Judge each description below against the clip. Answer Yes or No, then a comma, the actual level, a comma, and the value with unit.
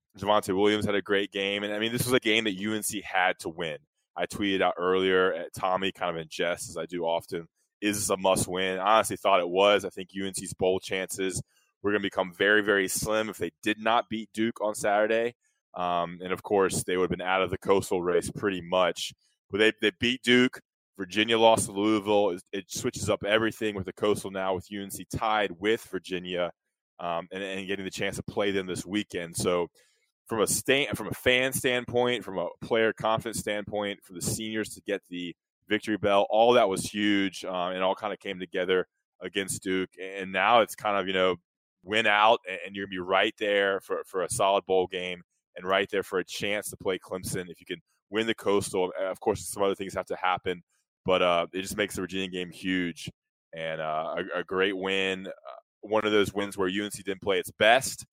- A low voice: Yes, low, 100 Hz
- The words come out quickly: Yes, fast, 220 wpm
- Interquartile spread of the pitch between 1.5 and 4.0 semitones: Yes, narrow, 2.4 semitones